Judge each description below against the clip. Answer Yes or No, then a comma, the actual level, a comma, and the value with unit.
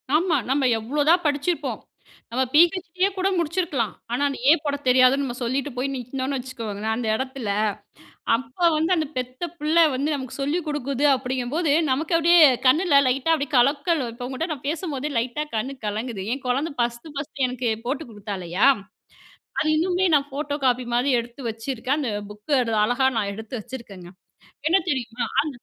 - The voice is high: Yes, very high, 270 Hz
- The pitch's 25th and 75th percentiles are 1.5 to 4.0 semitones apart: Yes, average, 3.7 semitones